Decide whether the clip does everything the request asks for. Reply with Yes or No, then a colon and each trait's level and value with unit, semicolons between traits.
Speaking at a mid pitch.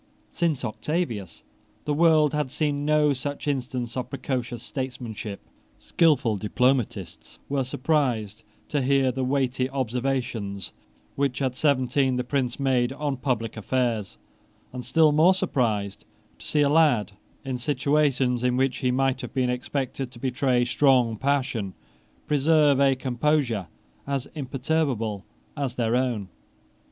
No: low, 130 Hz